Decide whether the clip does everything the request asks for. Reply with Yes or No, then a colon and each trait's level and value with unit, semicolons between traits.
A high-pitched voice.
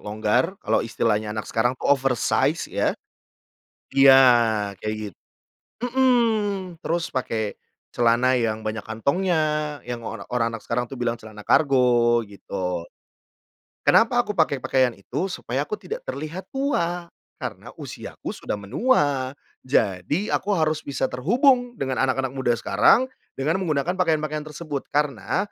No: low, 135 Hz